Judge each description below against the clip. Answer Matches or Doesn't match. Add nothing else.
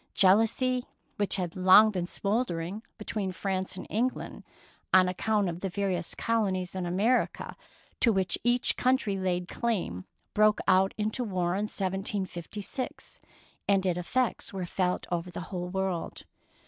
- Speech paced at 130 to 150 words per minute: Matches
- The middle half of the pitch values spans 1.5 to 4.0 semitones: Matches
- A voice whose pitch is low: Doesn't match